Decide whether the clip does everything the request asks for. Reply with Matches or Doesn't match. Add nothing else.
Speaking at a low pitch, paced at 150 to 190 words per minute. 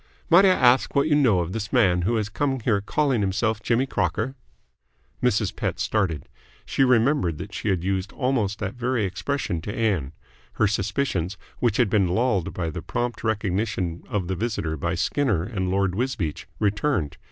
Matches